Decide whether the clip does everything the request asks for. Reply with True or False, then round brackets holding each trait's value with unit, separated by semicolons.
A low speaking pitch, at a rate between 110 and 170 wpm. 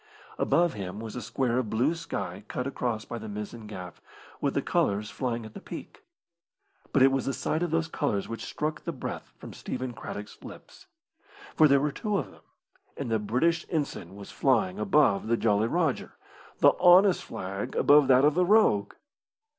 False (125 Hz; 185 wpm)